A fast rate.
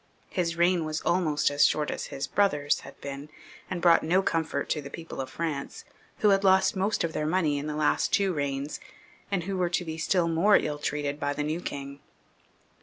Yes: fast, 210 wpm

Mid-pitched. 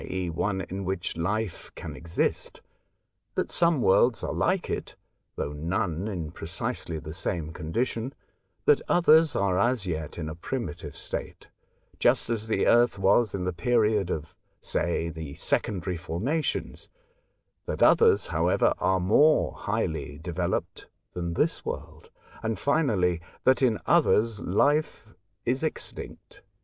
No: very low, 95 Hz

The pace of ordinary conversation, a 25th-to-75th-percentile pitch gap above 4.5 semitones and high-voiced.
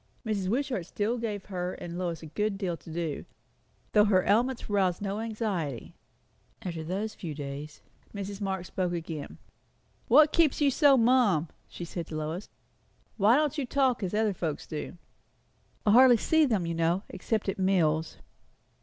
Yes: average, 165 wpm; average, 4.9 semitones; high, 195 Hz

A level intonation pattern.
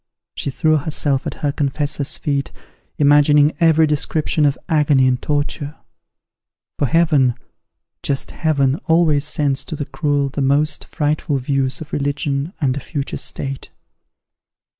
Yes: narrow, 1.7 semitones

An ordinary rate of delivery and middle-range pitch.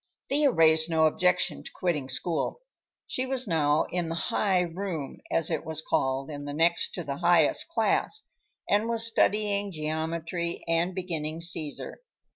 Yes: average, 150 wpm; medium, 165 Hz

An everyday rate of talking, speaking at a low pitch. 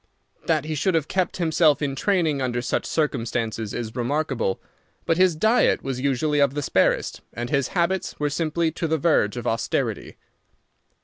No: average, 170 wpm; medium, 150 Hz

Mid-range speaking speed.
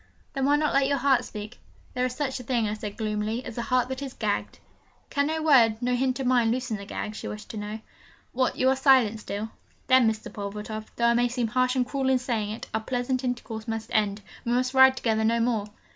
No: fast, 240 wpm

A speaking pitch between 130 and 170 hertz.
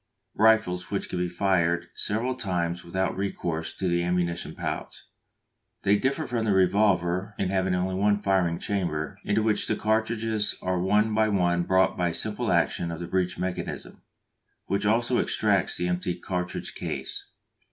No: very low, 95 Hz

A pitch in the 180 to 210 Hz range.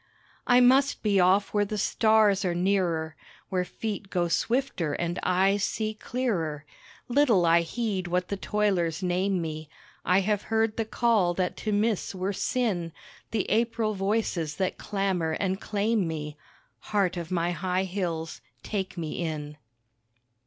Yes: high, 190 Hz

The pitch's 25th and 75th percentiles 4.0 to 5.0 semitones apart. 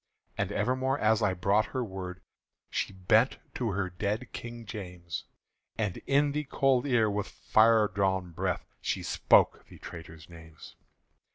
Yes: average, 4.6 semitones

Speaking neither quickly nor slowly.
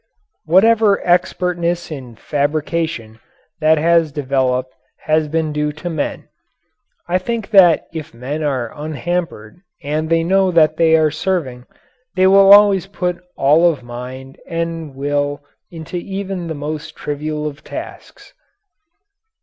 No: slow, 130 wpm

